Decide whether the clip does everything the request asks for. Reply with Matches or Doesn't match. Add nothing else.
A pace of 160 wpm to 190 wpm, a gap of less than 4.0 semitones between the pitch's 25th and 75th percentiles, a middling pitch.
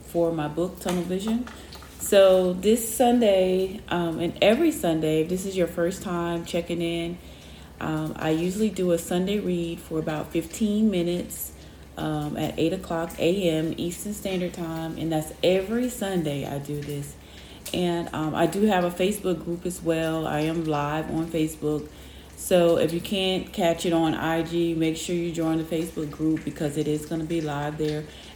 Matches